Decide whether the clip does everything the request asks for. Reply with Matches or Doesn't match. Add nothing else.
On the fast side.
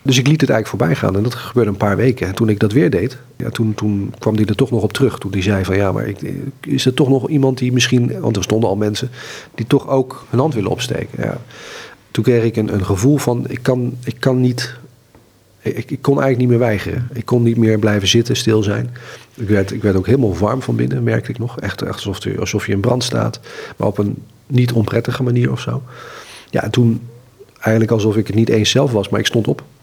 Matches